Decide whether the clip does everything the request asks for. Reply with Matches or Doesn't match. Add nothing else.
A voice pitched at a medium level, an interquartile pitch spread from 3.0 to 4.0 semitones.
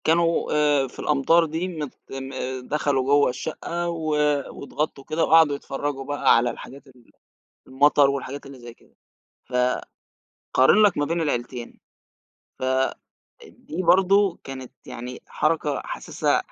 Matches